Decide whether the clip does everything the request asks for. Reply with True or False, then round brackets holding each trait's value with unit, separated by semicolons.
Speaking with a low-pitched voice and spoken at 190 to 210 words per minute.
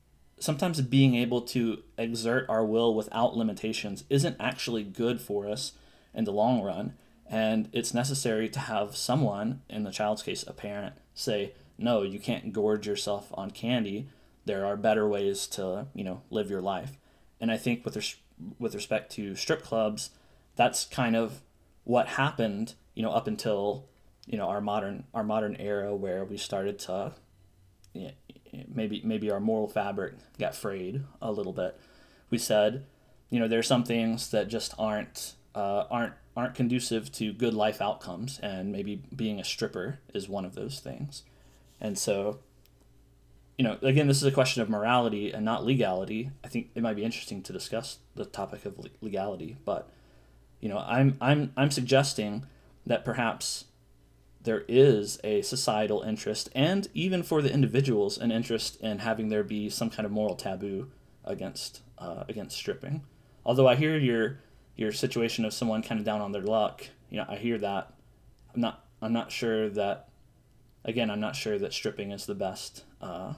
False (110 Hz; 175 wpm)